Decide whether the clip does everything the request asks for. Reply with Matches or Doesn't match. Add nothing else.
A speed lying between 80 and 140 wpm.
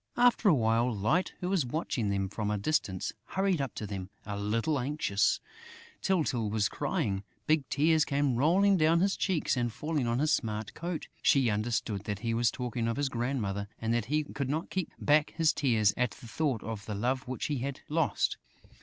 Doesn't match